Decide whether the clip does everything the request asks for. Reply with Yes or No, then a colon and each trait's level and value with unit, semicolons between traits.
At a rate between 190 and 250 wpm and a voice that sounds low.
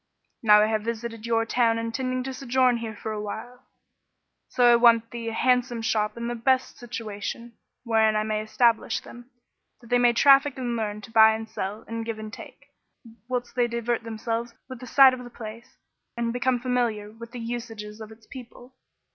No: average, 200 wpm; high, 235 Hz